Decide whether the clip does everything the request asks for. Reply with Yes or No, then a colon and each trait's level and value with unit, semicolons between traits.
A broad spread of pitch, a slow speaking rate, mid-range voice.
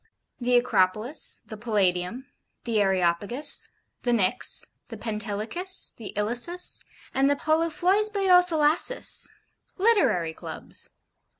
No: wide, 8.2 semitones; slow, 95 wpm; high, 245 Hz